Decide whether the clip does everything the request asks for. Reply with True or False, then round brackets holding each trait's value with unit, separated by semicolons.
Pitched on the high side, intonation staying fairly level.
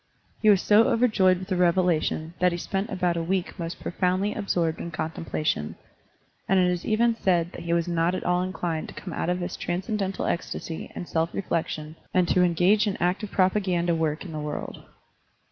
False (180 Hz; 2.2 semitones)